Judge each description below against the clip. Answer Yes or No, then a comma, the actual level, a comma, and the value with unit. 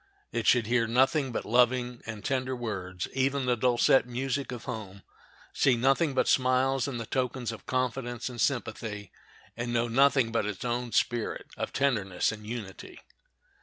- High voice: No, low, 120 Hz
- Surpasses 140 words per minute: Yes, average, 165 wpm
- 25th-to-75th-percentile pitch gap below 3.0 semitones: Yes, narrow, 2.4 semitones